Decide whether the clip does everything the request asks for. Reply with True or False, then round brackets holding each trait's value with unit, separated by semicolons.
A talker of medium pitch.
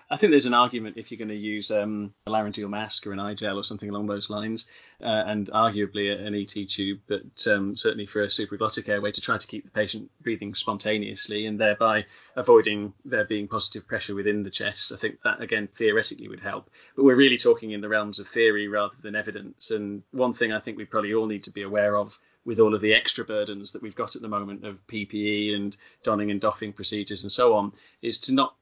False (105 Hz)